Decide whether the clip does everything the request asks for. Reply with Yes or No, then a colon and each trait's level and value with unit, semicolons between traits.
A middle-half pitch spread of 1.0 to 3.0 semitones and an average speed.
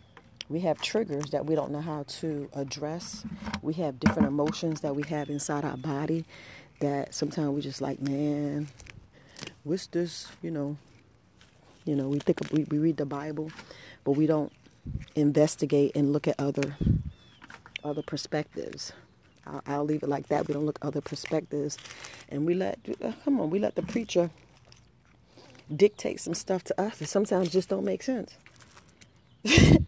Yes: average, 2.7 semitones; average, 165 wpm